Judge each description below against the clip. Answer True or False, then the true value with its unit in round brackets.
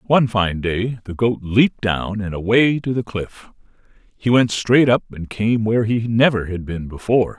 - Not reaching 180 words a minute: False (195 wpm)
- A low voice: True (110 Hz)